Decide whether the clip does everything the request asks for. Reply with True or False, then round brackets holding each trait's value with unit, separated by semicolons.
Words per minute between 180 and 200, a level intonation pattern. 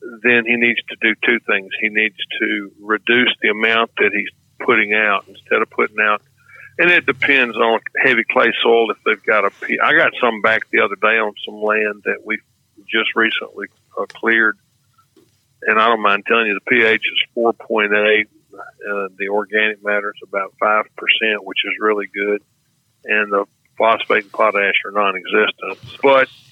True (185 wpm; 2.3 semitones)